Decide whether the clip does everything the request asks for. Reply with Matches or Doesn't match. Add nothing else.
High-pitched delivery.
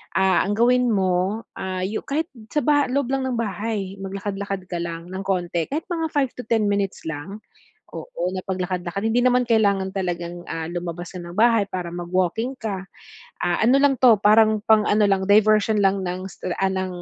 Matches